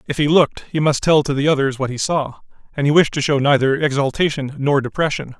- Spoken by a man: Yes, male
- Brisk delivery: Yes, fast, 235 wpm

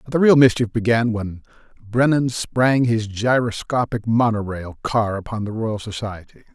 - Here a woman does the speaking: No, male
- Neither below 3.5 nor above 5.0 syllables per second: Yes, 4.6 syllables/s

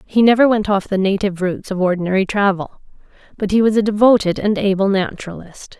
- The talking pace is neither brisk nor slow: Yes, average, 185 wpm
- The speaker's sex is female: Yes, female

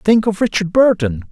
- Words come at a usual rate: Yes, average, 180 wpm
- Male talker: Yes, male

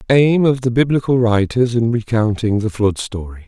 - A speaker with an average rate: Yes, average, 175 wpm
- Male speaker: Yes, male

